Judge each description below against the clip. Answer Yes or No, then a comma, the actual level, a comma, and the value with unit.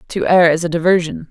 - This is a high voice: No, medium, 170 Hz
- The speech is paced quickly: Yes, fast, 230 wpm